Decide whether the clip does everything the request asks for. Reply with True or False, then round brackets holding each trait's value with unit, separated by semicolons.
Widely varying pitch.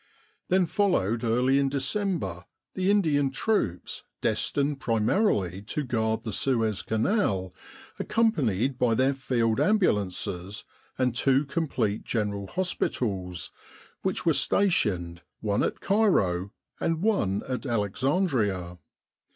True (7.7 semitones)